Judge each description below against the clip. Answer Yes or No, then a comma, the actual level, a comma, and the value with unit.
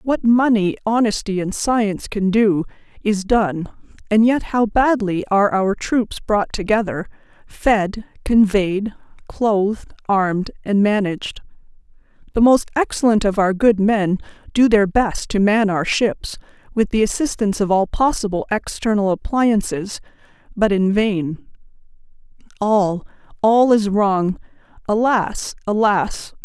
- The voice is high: Yes, high, 210 Hz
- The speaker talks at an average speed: No, slow, 125 wpm